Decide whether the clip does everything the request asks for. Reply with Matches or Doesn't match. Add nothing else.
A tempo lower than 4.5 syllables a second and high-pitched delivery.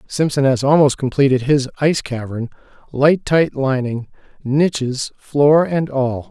Doesn't match